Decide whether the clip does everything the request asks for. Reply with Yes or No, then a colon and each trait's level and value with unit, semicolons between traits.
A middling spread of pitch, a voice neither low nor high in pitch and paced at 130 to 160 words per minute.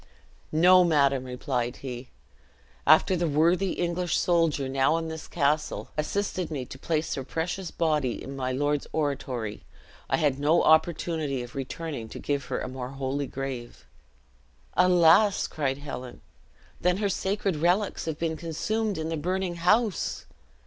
Yes: average, 4.3 semitones; medium, 155 Hz; average, 150 wpm